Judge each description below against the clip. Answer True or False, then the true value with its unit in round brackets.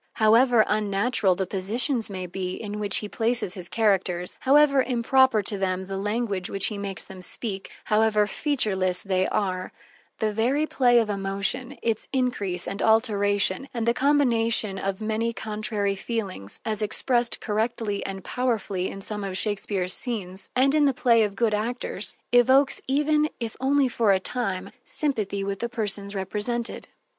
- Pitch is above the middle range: True (215 Hz)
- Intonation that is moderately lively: True (3.7 semitones)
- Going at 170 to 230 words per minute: False (160 wpm)